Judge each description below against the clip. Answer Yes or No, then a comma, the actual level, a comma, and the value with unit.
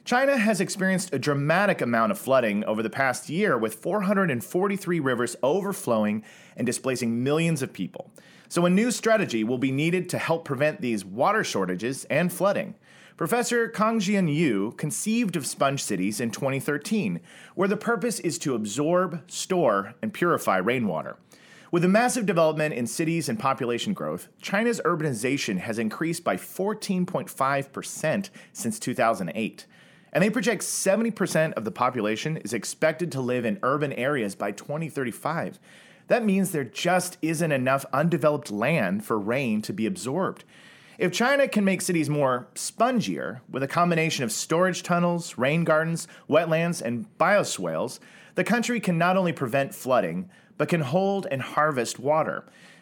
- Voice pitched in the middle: Yes, medium, 165 Hz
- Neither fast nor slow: Yes, average, 150 wpm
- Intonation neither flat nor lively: No, wide, 6.4 semitones